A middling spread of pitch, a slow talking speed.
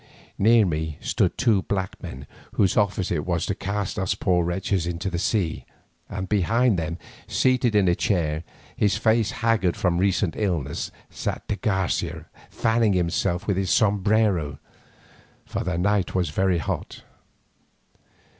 No: average, 3.1 semitones; average, 145 wpm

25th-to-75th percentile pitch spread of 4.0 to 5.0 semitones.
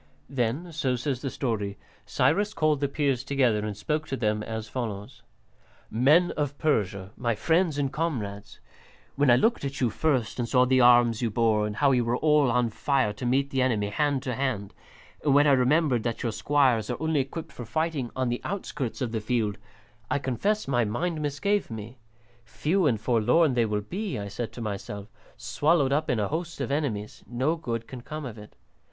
Yes: average, 4.7 semitones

